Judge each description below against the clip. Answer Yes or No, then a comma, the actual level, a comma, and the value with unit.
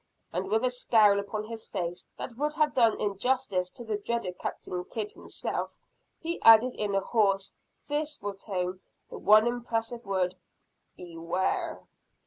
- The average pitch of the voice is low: No, high, 215 Hz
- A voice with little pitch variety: No, average, 3.8 semitones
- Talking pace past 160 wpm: No, average, 150 wpm